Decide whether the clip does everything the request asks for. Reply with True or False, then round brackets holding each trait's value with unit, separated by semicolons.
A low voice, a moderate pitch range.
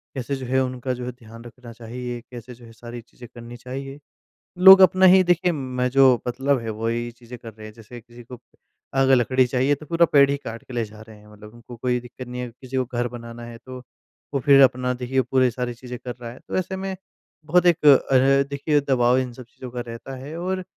False (125 Hz; 2.3 semitones)